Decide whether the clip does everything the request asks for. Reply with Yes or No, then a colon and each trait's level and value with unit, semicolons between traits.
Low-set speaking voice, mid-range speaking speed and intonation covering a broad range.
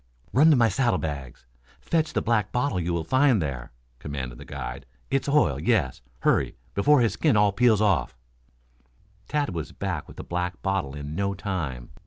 Yes: very low, 95 Hz; average, 175 wpm; wide, 9.0 semitones